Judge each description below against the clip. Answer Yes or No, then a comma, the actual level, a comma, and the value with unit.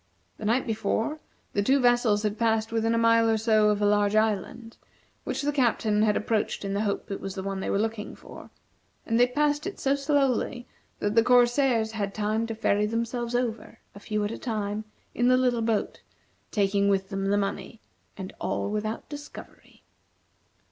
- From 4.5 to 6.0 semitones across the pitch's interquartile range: No, average, 2.7 semitones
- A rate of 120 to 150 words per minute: No, average, 190 wpm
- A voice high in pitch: Yes, high, 220 Hz